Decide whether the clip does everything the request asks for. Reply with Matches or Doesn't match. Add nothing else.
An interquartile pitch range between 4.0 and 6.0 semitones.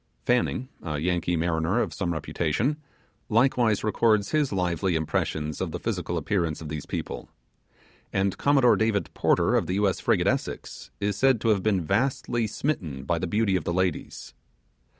Matches